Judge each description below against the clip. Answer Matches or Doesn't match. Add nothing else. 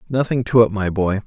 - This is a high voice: Doesn't match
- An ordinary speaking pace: Doesn't match